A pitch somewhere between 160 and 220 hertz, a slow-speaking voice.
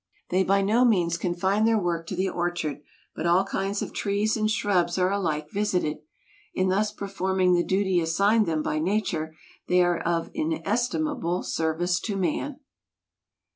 No: high, 190 Hz; average, 160 wpm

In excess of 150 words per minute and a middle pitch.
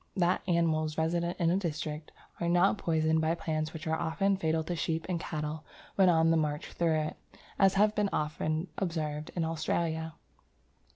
Yes: average, 170 wpm; medium, 160 Hz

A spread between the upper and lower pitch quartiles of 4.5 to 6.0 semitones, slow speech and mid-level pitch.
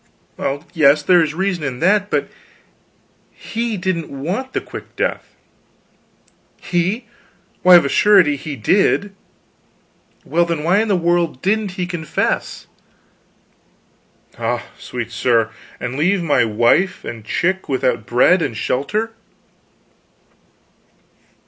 Yes: wide, 5.6 semitones; slow, 120 wpm; medium, 170 Hz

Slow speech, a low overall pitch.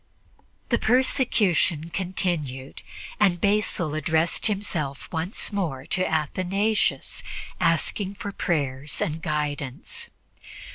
No: slow, 90 wpm; medium, 170 Hz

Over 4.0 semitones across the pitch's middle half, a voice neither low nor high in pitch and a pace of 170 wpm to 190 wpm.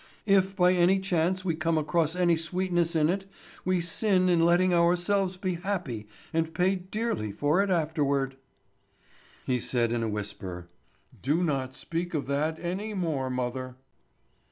No: average, 4.7 semitones; medium, 170 Hz; average, 155 wpm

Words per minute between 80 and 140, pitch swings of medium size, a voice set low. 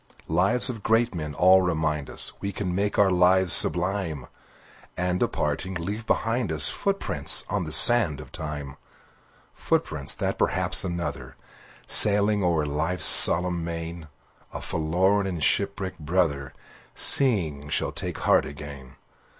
Yes: slow, 135 wpm; average, 4.4 semitones; very low, 90 Hz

